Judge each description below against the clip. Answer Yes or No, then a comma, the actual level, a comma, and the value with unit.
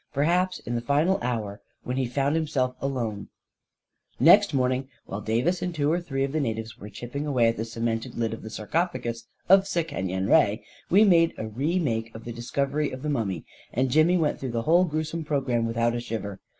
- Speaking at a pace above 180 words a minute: Yes, fast, 205 wpm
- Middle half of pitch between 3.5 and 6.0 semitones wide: Yes, average, 5.2 semitones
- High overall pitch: No, low, 130 Hz